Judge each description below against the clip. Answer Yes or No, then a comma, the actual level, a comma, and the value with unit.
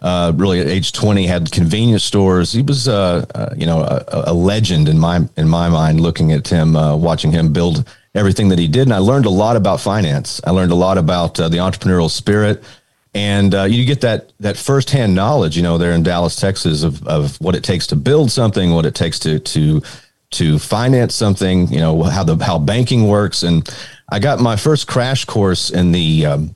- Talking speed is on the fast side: Yes, fast, 215 wpm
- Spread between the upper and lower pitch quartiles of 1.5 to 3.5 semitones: No, average, 4.5 semitones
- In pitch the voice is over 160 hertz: No, very low, 95 Hz